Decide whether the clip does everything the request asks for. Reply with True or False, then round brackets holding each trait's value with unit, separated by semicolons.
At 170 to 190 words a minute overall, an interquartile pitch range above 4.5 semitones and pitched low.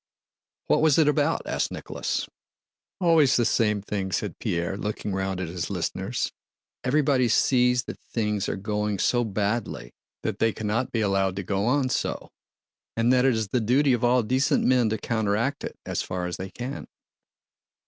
False (175 wpm; 4.2 semitones; 110 Hz)